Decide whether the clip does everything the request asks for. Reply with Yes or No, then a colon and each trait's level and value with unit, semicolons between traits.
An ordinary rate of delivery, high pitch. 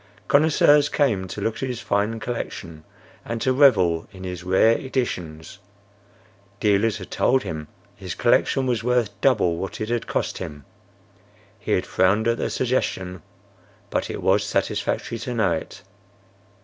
No: average, 150 wpm; low, 110 Hz